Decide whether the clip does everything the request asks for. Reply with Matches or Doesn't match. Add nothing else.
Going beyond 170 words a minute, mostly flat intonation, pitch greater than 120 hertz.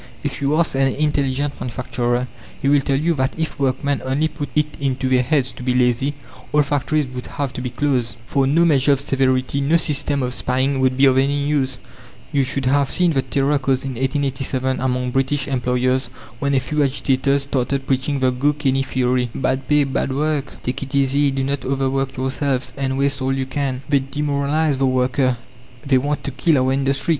Matches